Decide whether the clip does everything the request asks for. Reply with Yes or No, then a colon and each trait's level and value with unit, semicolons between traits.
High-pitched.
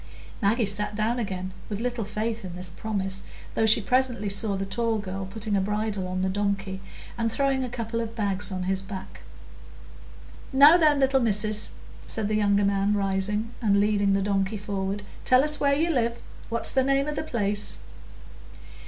Yes: high, 210 Hz